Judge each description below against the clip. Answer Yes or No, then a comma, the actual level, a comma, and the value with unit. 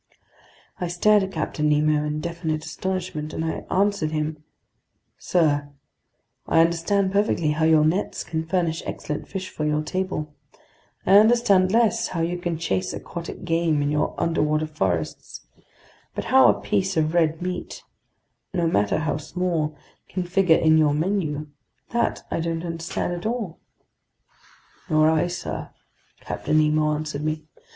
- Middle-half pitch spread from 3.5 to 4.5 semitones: No, average, 2.9 semitones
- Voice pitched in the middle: Yes, medium, 160 Hz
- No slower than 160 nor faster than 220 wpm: No, average, 145 wpm